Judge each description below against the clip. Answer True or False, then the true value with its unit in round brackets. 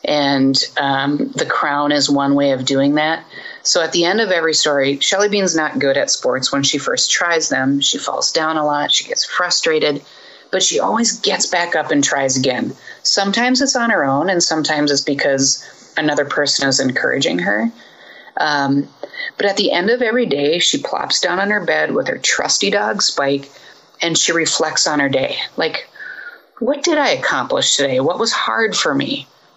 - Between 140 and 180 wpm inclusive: False (195 wpm)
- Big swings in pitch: True (6.1 semitones)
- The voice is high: False (145 Hz)